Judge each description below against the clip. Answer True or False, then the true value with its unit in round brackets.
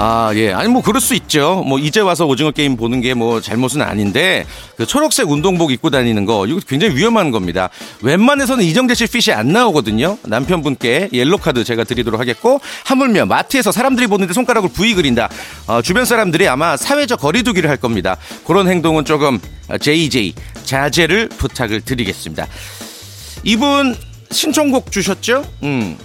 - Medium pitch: True (150 Hz)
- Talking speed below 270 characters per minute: False (375 characters per minute)